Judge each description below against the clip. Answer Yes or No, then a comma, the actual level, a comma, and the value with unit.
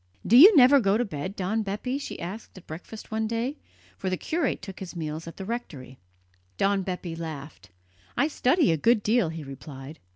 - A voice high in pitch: Yes, high, 195 Hz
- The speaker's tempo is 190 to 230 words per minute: Yes, average, 195 wpm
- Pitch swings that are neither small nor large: No, wide, 6.4 semitones